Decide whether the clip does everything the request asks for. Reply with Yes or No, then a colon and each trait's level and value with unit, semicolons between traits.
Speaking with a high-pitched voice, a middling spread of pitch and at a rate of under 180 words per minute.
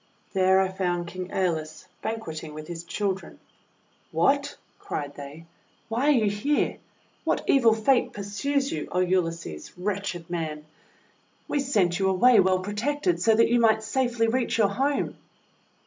Yes: high, 195 Hz; average, 4.8 semitones; average, 150 wpm